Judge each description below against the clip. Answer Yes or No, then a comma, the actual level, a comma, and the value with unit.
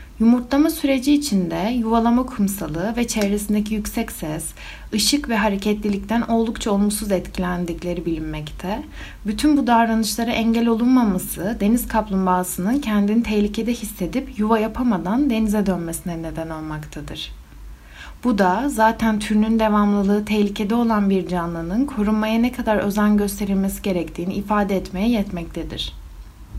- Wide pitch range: No, average, 3.9 semitones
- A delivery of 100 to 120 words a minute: Yes, average, 115 wpm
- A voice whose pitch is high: Yes, high, 210 Hz